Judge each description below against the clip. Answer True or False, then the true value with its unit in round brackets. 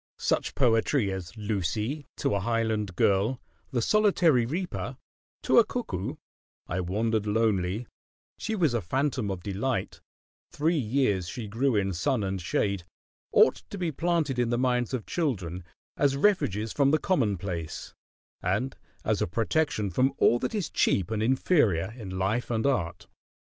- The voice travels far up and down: True (5.9 semitones)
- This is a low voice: True (115 Hz)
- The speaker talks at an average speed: True (155 wpm)